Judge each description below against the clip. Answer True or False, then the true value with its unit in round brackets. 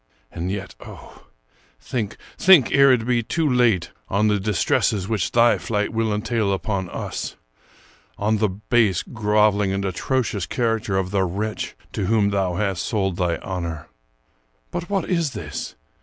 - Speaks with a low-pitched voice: True (105 Hz)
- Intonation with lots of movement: False (3.2 semitones)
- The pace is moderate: True (160 wpm)